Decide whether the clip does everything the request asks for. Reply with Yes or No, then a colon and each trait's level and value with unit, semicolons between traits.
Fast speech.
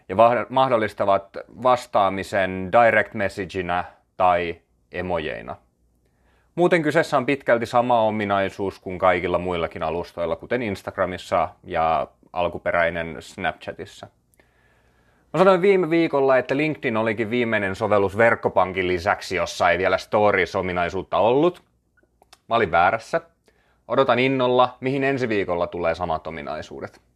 No: average, 105 wpm